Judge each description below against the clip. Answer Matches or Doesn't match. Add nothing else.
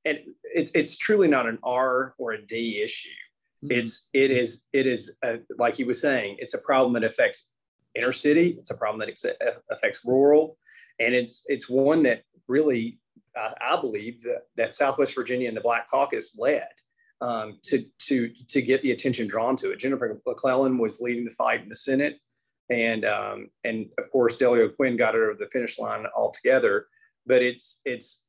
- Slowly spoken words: Doesn't match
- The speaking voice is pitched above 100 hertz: Matches